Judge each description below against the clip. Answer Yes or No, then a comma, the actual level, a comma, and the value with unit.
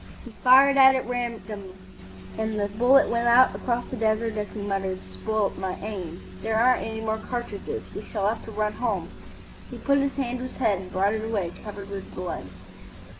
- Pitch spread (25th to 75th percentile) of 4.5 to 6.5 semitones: No, average, 3.4 semitones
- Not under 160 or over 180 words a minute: No, average, 195 wpm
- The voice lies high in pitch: Yes, high, 220 Hz